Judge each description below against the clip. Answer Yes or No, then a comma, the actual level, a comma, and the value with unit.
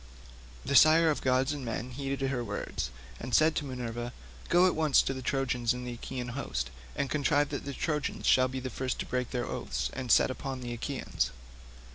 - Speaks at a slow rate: No, average, 200 wpm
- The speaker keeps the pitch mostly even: Yes, narrow, 2.3 semitones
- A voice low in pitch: Yes, low, 130 Hz